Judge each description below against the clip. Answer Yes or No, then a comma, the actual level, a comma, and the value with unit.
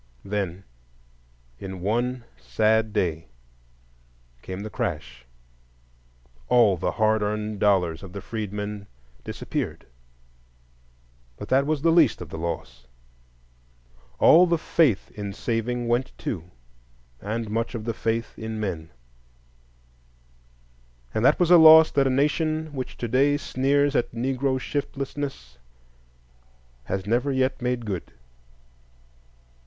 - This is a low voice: Yes, low, 110 Hz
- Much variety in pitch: Yes, wide, 8.1 semitones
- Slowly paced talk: Yes, slow, 115 wpm